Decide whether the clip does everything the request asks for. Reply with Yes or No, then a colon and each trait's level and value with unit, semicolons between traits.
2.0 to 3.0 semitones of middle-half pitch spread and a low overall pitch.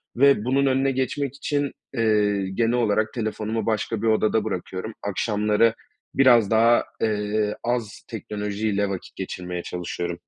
Yes: narrow, 2.5 semitones; low, 110 Hz